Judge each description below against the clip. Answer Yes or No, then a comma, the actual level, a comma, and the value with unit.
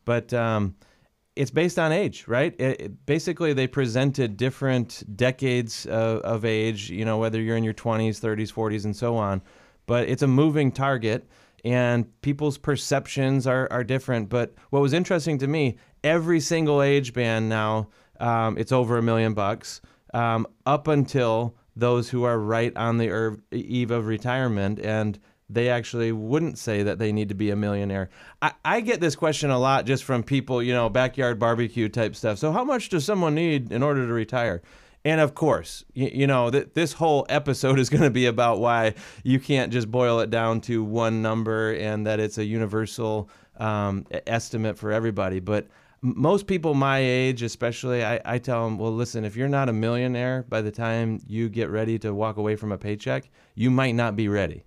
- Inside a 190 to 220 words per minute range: Yes, average, 195 wpm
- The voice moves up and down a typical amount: Yes, average, 3.3 semitones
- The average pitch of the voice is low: Yes, low, 120 Hz